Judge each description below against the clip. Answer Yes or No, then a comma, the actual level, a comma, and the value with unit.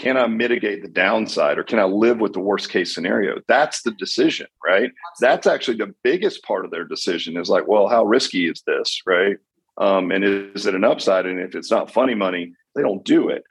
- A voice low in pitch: Yes, low, 120 Hz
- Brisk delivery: Yes, fast, 220 wpm